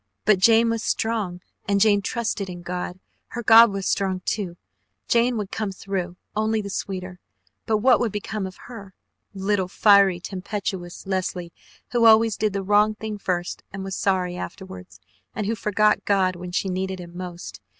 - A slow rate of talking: No, average, 170 wpm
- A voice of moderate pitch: No, high, 195 Hz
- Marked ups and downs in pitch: No, average, 2.7 semitones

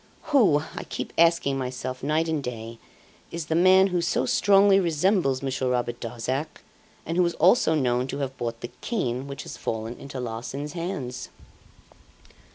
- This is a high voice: No, medium, 140 Hz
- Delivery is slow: No, average, 165 wpm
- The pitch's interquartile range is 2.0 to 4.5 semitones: No, average, 5.3 semitones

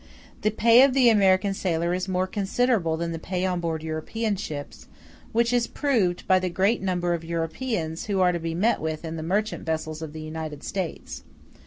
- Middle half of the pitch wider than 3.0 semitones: Yes, average, 4.4 semitones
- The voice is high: No, medium, 180 Hz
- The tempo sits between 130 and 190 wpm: No, average, 200 wpm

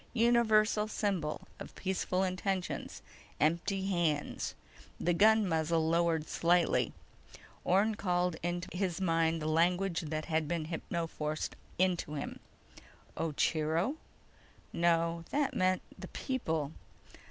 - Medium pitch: Yes, medium, 175 Hz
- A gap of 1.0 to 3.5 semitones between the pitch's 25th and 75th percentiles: Yes, average, 2.9 semitones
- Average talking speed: No, slow, 105 wpm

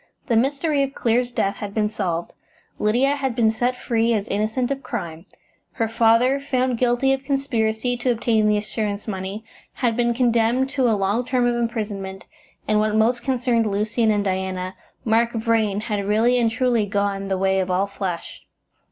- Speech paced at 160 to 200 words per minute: Yes, average, 180 wpm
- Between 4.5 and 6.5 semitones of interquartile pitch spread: No, average, 3.3 semitones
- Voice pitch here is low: No, high, 225 Hz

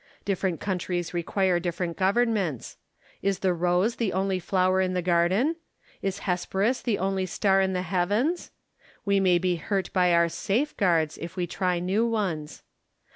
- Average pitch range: No, narrow, 2.1 semitones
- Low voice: No, medium, 185 Hz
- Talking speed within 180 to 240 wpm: No, average, 155 wpm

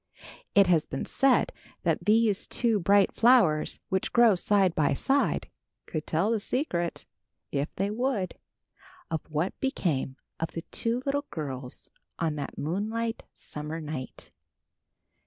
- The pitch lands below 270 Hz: Yes, high, 190 Hz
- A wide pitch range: Yes, wide, 6.7 semitones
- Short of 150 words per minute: Yes, slow, 135 wpm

